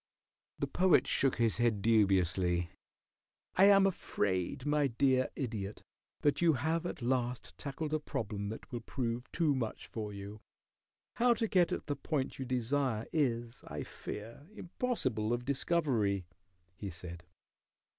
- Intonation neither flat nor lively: No, wide, 5.7 semitones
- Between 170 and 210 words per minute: No, average, 145 wpm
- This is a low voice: Yes, low, 125 Hz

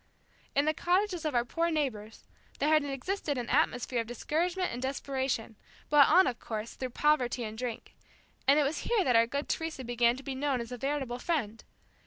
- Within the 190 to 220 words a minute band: Yes, average, 200 wpm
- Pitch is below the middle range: No, very high, 270 Hz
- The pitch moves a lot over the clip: No, average, 4.2 semitones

